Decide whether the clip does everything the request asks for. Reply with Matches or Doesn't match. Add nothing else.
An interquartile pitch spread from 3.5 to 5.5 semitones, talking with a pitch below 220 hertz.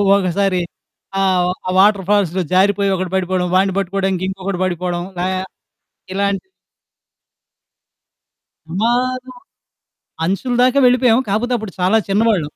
Doesn't match